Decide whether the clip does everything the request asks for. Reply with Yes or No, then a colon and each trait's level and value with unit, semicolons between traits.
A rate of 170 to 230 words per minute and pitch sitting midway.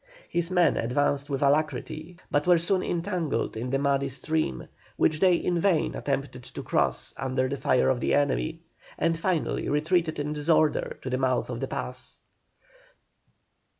No: average, 160 wpm; medium, 145 Hz